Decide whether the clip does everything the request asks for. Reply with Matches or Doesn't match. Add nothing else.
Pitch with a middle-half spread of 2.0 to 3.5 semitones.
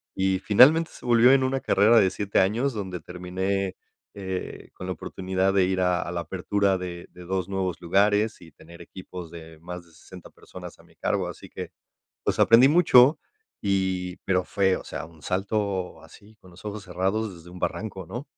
Matches